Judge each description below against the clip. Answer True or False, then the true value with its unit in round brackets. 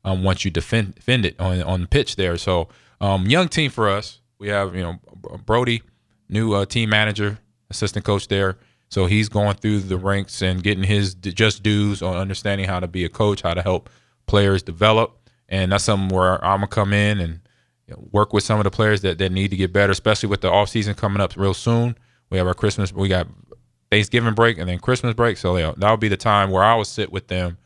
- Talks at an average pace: False (235 wpm)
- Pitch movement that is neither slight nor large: False (2.2 semitones)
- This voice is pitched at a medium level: False (100 Hz)